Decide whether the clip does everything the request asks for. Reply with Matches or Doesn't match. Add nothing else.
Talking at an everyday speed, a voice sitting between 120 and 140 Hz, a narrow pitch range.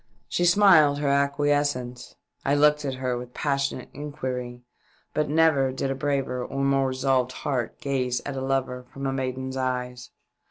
Matches